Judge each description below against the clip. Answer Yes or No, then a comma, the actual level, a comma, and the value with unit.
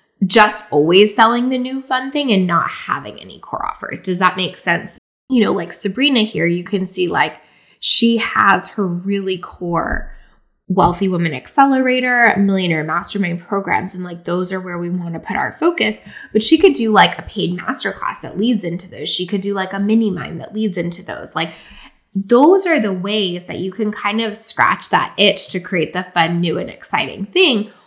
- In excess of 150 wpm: Yes, average, 200 wpm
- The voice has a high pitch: Yes, high, 200 Hz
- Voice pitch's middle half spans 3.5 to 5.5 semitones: Yes, average, 4.0 semitones